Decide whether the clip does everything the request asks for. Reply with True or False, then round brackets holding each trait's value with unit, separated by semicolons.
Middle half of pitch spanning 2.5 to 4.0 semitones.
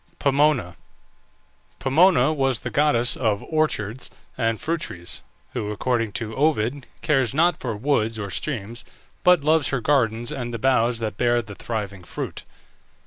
False (4.7 semitones)